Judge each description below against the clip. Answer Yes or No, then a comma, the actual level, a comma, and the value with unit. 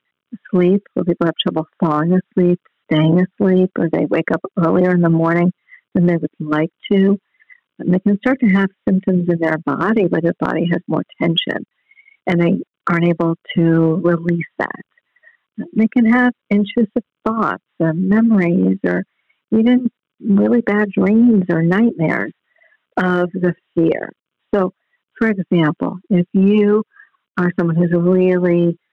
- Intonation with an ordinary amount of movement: Yes, average, 3.8 semitones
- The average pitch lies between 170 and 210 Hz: Yes, medium, 185 Hz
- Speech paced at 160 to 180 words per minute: No, average, 145 wpm